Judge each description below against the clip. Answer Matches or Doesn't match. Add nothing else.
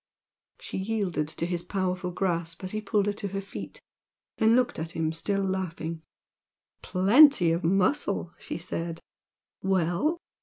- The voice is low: Doesn't match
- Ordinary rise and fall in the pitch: Matches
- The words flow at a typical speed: Matches